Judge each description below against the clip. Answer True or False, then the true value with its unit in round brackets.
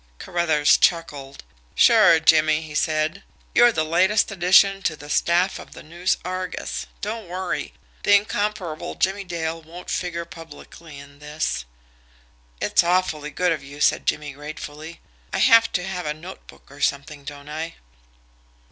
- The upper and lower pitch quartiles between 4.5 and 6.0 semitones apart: False (3.3 semitones)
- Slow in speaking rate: False (145 wpm)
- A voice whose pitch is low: False (165 Hz)